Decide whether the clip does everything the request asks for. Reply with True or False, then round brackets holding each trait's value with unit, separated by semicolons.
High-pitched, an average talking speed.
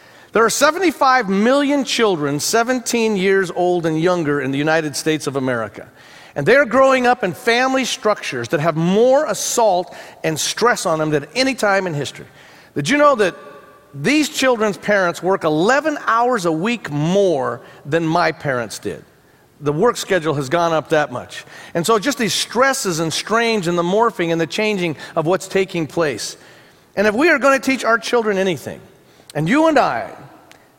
True (195 Hz; 180 wpm)